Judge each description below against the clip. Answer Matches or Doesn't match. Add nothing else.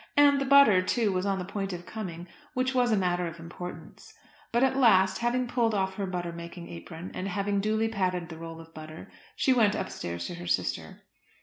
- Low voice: Doesn't match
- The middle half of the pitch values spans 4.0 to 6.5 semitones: Matches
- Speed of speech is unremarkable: Doesn't match